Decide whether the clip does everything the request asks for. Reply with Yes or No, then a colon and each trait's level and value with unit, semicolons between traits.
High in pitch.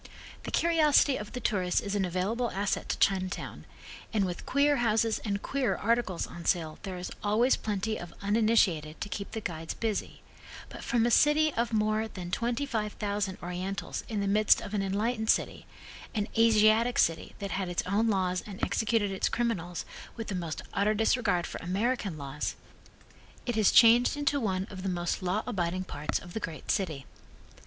Yes: high, 205 Hz